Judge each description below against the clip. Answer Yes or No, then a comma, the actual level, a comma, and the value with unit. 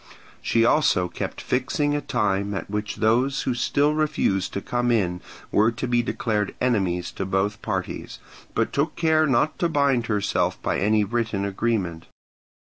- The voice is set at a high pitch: No, low, 115 Hz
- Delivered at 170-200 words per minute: No, average, 160 wpm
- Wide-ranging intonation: No, average, 4.6 semitones